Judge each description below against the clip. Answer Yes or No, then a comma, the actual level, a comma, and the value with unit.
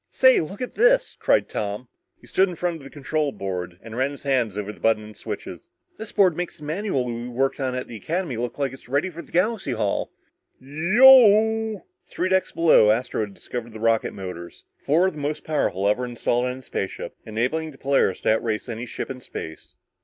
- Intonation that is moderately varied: No, wide, 7.3 semitones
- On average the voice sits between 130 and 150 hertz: Yes, low, 135 Hz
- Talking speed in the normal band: No, fast, 210 wpm